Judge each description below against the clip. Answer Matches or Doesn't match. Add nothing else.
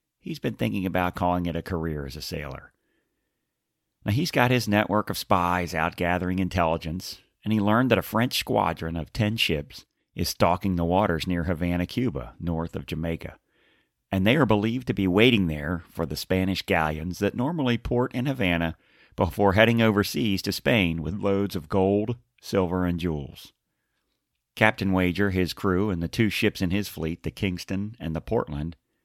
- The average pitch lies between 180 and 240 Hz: Doesn't match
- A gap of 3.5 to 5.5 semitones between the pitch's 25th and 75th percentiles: Matches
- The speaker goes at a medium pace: Matches